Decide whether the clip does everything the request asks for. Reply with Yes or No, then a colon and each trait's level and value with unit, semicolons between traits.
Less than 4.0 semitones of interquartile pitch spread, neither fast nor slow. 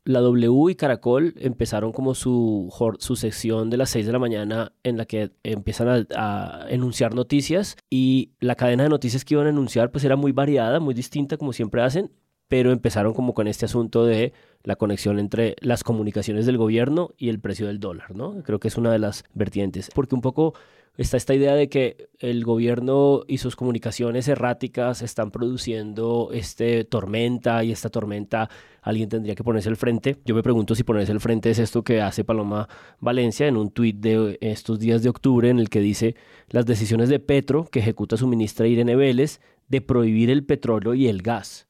No: narrow, 2.5 semitones; fast, 195 wpm